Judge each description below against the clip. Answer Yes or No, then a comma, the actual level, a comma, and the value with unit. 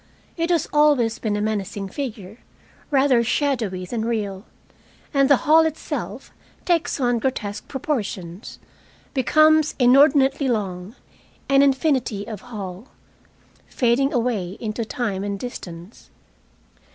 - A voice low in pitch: No, high, 240 Hz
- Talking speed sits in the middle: No, slow, 115 wpm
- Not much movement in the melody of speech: No, average, 5.2 semitones